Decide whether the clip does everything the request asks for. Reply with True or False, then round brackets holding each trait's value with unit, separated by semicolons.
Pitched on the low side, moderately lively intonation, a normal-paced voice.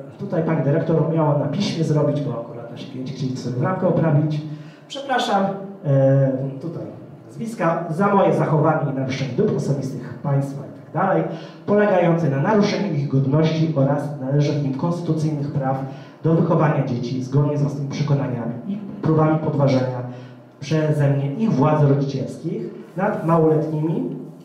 False (150 Hz; 3.3 semitones; 135 wpm)